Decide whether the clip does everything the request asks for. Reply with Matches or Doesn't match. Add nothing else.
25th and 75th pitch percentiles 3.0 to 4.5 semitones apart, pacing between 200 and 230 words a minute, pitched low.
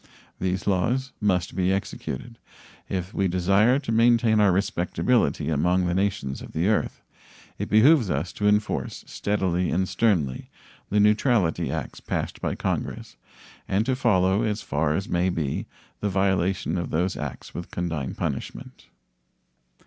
Doesn't match